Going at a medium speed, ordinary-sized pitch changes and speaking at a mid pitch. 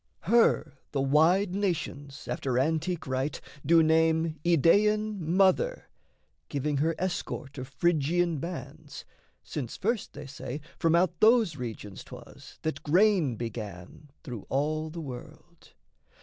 No: slow, 120 wpm; average, 4.2 semitones; medium, 160 Hz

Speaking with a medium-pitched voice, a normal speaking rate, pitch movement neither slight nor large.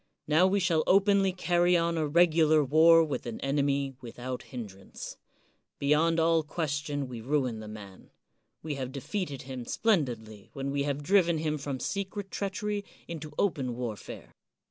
Yes: medium, 150 Hz; average, 155 wpm; average, 4.6 semitones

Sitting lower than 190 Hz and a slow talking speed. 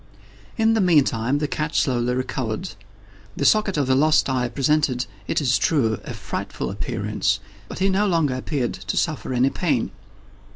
No: low, 135 Hz; average, 165 wpm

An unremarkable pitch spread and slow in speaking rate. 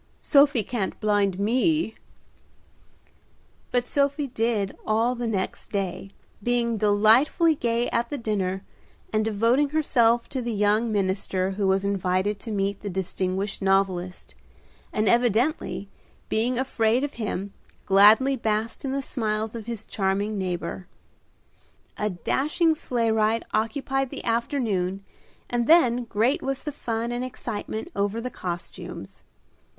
Yes: average, 3.6 semitones; slow, 130 wpm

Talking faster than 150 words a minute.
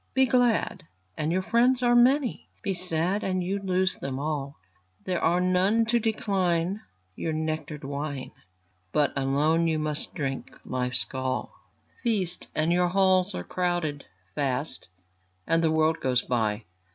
No: average, 145 wpm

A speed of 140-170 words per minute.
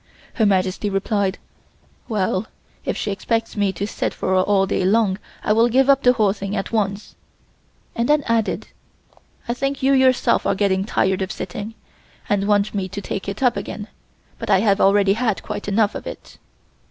No: average, 190 wpm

